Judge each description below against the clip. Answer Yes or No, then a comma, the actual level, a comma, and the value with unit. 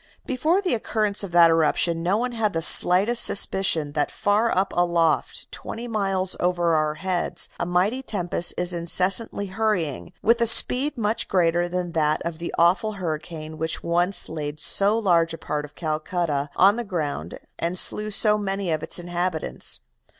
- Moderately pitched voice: Yes, medium, 180 Hz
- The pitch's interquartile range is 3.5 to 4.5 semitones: Yes, average, 4.0 semitones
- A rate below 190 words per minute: Yes, average, 170 wpm